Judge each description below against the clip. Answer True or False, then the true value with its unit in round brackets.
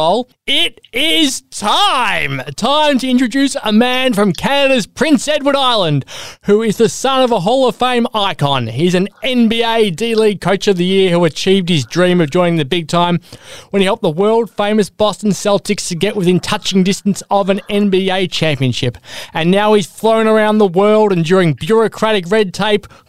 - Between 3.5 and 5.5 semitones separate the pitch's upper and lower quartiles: True (3.9 semitones)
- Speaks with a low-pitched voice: False (205 Hz)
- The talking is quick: False (180 wpm)